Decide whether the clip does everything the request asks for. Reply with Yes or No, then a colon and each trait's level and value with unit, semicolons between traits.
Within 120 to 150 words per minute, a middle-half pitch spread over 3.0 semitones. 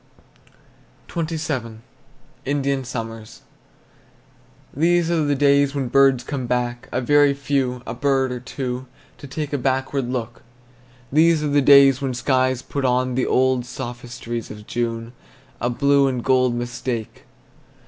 No: average, 140 wpm; narrow, 2.5 semitones